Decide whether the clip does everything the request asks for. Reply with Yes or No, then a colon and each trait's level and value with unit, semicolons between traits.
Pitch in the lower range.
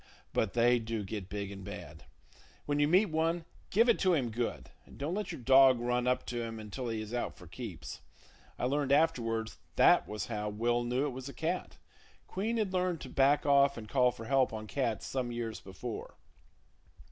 Yes: low, 125 Hz